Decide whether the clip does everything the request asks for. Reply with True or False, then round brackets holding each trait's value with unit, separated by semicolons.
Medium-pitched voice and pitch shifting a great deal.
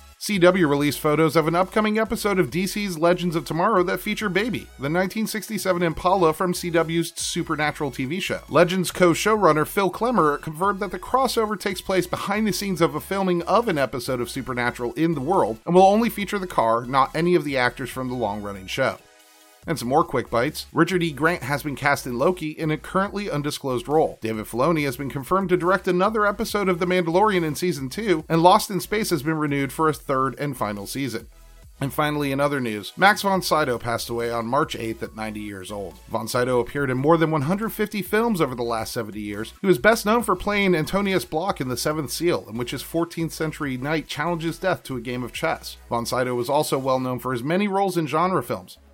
True (160 Hz; 6.1 semitones)